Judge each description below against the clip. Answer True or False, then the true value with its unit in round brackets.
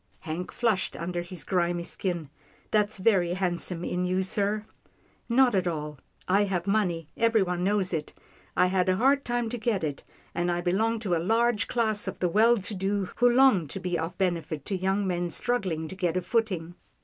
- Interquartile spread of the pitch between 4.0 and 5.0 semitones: False (3.6 semitones)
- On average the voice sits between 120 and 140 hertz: False (185 Hz)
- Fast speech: True (210 wpm)